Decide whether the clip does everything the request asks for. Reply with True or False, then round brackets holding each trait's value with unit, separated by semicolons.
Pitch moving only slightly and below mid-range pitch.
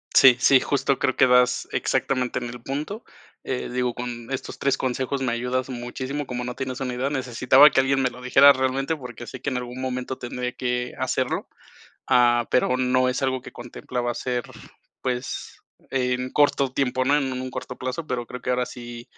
True (1.2 semitones; 125 Hz)